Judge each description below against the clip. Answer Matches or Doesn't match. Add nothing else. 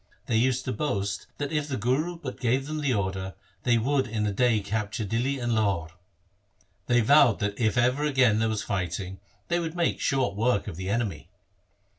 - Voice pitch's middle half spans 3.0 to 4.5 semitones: Doesn't match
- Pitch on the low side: Matches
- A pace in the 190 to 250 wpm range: Matches